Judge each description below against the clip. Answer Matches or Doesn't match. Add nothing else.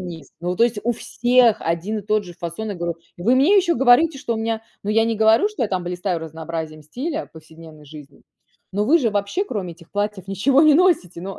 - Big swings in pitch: Matches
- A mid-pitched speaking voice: Doesn't match